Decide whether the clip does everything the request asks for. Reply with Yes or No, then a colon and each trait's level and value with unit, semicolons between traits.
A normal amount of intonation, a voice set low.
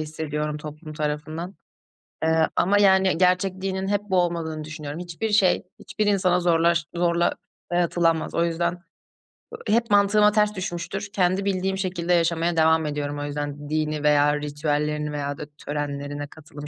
No: average, 3.8 semitones; medium, 170 Hz